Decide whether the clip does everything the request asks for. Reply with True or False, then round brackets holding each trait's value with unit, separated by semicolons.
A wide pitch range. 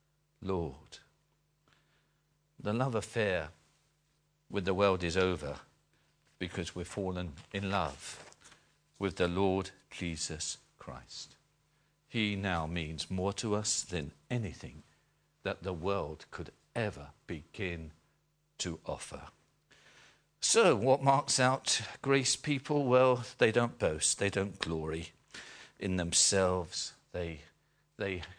True (6.3 semitones)